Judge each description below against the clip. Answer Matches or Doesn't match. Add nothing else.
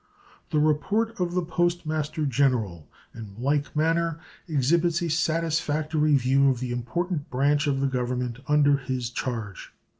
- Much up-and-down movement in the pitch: Doesn't match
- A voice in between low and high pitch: Matches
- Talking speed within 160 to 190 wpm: Doesn't match